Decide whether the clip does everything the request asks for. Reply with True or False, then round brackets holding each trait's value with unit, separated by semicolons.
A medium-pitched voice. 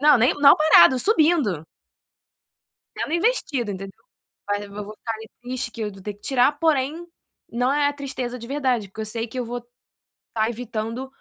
False (245 Hz)